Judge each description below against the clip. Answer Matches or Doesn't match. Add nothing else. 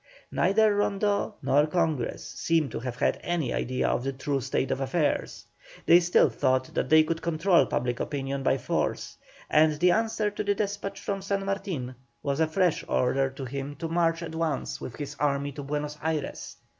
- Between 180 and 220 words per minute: Matches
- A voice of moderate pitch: Matches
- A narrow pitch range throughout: Doesn't match